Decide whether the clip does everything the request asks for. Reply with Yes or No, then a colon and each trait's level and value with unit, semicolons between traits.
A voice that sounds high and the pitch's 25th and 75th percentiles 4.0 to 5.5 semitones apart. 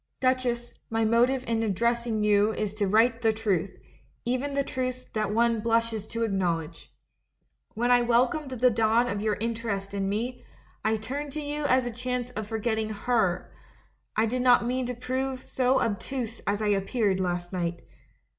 No: high, 230 Hz; average, 3.0 semitones